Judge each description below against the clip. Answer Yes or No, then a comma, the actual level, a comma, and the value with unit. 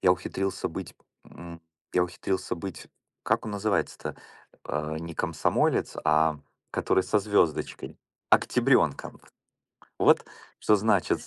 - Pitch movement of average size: Yes, average, 3.3 semitones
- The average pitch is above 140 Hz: No, very low, 90 Hz